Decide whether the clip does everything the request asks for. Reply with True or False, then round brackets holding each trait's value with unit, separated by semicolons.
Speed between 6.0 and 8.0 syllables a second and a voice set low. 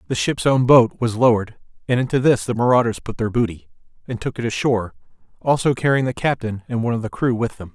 True (6.4 syllables/s; 120 Hz)